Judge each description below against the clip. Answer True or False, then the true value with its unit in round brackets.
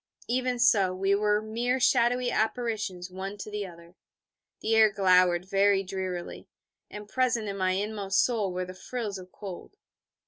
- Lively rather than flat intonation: False (3.2 semitones)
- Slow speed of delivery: False (160 wpm)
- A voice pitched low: False (200 Hz)